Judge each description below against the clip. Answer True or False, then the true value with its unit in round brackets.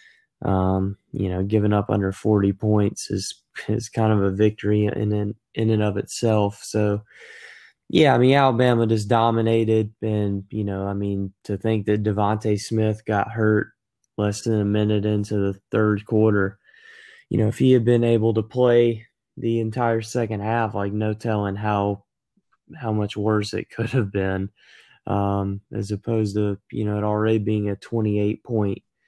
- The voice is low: True (105 Hz)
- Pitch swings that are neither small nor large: False (1.6 semitones)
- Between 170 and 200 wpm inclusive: True (175 wpm)